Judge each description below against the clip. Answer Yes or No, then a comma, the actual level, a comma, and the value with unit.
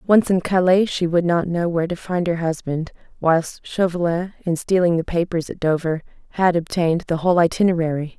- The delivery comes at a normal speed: Yes, average, 185 wpm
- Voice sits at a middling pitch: Yes, medium, 170 Hz